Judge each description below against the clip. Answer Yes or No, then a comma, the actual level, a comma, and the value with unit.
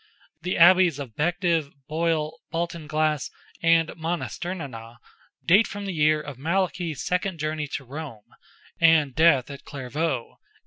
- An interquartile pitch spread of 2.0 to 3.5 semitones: Yes, average, 2.8 semitones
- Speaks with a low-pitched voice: No, medium, 160 Hz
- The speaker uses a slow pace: Yes, slow, 125 wpm